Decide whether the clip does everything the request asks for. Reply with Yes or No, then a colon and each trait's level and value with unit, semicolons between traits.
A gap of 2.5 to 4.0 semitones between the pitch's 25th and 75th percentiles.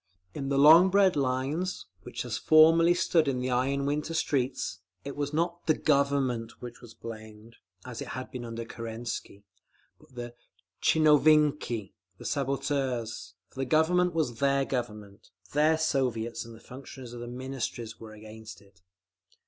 No: average, 4.5 semitones